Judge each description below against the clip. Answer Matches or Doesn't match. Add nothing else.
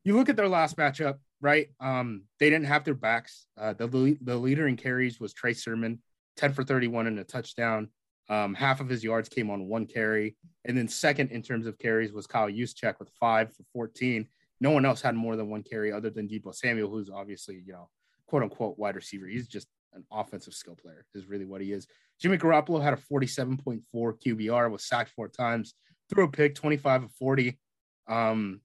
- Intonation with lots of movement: Doesn't match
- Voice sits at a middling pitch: Doesn't match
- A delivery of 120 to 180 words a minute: Doesn't match